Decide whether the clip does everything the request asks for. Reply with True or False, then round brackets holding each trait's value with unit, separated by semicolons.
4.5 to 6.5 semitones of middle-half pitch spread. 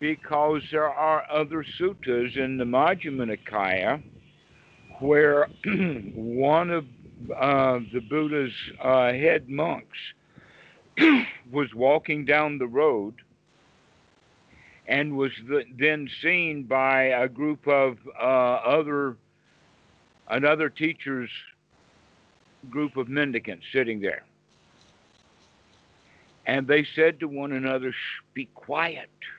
False (2.8 semitones)